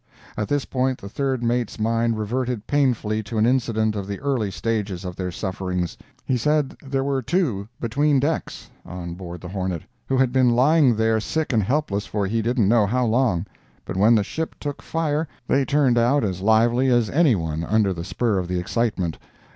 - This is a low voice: Yes, low, 115 Hz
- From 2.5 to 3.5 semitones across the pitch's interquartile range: No, average, 5.0 semitones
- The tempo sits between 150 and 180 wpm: No, average, 195 wpm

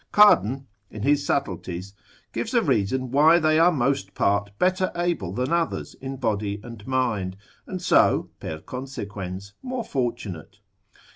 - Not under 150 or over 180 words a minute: No, average, 140 wpm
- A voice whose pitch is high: No, low, 125 Hz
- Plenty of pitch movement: Yes, wide, 7.3 semitones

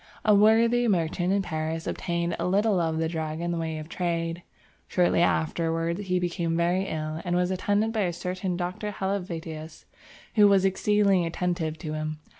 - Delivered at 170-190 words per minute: Yes, average, 175 wpm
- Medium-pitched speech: Yes, medium, 175 Hz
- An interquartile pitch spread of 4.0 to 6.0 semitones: No, average, 2.8 semitones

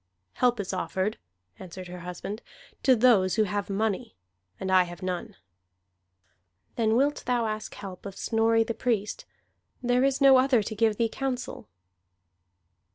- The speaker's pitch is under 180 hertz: No, high, 220 Hz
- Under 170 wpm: Yes, average, 150 wpm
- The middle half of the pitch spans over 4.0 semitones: Yes, average, 4.4 semitones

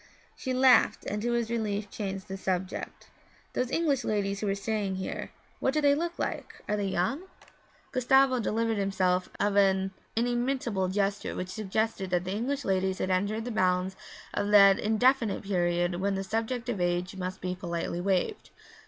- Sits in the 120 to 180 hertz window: No, high, 200 Hz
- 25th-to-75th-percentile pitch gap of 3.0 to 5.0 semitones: Yes, average, 3.9 semitones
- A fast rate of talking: No, average, 170 wpm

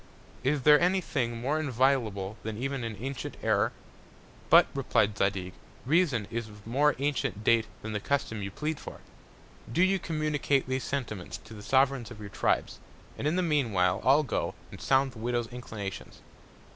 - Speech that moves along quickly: No, average, 175 wpm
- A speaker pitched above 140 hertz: No, low, 125 Hz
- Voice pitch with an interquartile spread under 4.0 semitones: No, average, 4.8 semitones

